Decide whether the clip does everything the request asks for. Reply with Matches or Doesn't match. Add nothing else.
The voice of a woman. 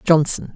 Matches